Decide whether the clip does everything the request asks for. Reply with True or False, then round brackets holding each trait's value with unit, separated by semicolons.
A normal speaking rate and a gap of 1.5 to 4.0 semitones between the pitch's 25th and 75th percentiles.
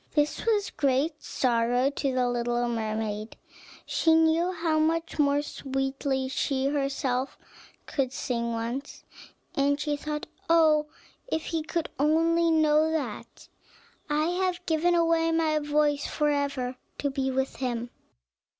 False (130 wpm; 3.6 semitones)